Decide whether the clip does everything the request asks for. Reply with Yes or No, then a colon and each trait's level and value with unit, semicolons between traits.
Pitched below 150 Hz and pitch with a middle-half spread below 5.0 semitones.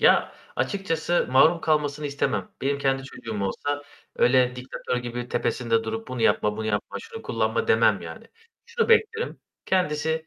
No: medium, 140 Hz; average, 5.3 semitones